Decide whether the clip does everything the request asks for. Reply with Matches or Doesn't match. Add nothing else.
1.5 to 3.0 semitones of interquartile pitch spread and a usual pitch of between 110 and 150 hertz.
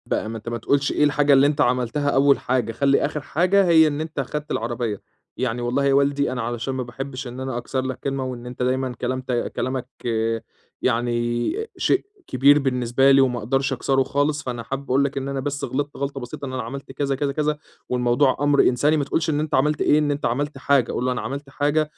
Matches